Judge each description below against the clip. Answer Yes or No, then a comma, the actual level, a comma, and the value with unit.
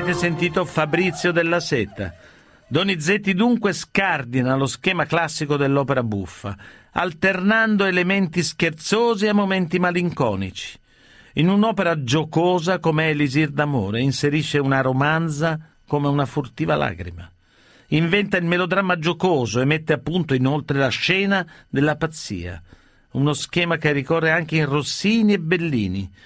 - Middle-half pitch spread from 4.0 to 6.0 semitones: Yes, average, 4.7 semitones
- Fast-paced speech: No, average, 125 wpm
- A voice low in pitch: No, medium, 160 Hz